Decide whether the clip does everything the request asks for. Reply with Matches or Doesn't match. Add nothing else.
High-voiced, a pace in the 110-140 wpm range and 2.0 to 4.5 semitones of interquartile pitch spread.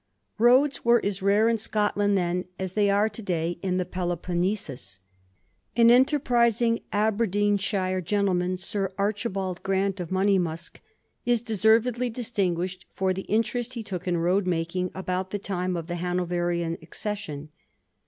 Matches